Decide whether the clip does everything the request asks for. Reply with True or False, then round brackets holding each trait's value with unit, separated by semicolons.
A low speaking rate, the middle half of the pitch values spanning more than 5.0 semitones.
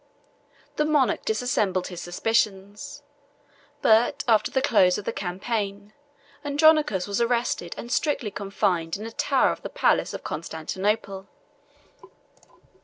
False (120 wpm; 3.8 semitones)